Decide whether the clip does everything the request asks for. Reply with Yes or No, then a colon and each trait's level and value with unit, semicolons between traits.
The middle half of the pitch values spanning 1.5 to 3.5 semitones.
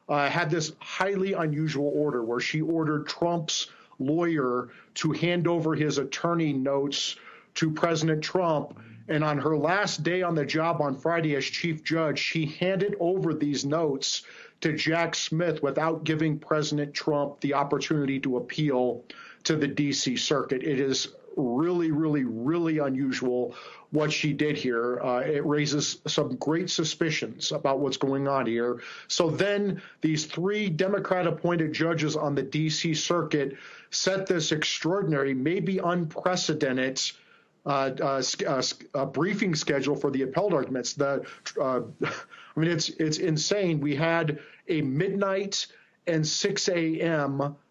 Yes: average, 3.1 semitones